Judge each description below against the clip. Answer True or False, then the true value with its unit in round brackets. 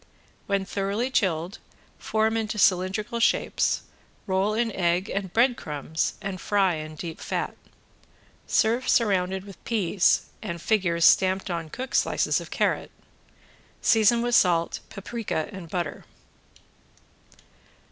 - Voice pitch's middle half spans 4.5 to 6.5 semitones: False (4.0 semitones)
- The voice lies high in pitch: True (195 Hz)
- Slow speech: True (120 wpm)